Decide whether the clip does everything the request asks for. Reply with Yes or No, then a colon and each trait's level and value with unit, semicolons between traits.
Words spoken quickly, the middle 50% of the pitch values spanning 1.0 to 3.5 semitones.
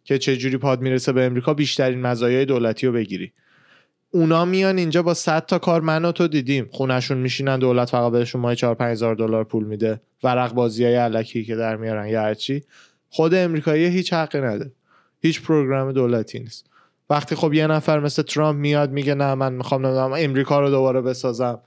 No: fast, 185 wpm; average, 4.1 semitones